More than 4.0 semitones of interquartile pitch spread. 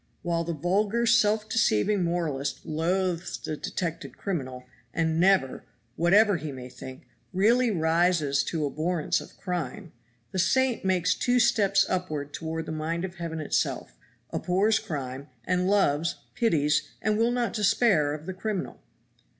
Yes: average, 4.6 semitones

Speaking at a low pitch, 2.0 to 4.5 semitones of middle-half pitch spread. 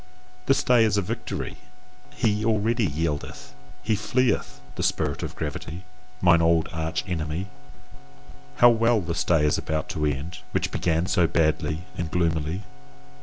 No: very low, 85 Hz; average, 4.9 semitones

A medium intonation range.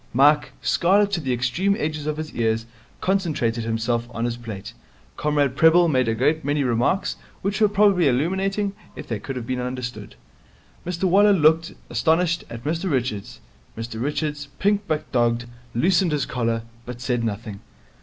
No: wide, 6.2 semitones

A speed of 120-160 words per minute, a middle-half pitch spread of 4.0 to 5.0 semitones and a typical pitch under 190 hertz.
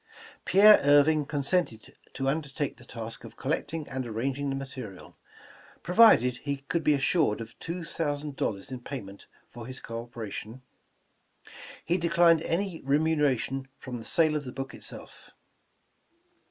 Yes: average, 140 wpm; average, 4.7 semitones; medium, 140 Hz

